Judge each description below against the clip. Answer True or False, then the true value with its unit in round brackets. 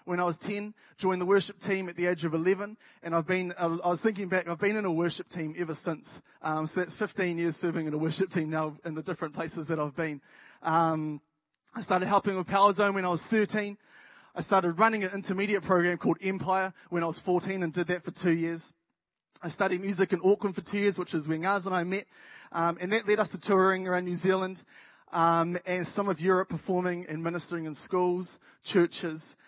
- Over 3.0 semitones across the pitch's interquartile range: False (2.7 semitones)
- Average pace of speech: False (225 wpm)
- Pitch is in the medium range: True (180 Hz)